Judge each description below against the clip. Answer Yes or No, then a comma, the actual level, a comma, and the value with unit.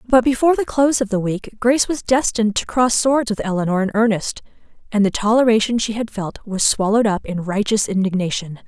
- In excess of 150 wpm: Yes, average, 200 wpm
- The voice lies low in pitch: No, high, 220 Hz